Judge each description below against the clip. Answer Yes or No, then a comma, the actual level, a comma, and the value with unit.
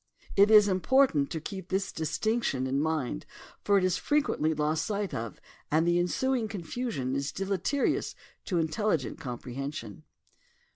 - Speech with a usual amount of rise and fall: No, wide, 6.3 semitones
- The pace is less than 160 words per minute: Yes, average, 150 wpm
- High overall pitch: No, medium, 175 Hz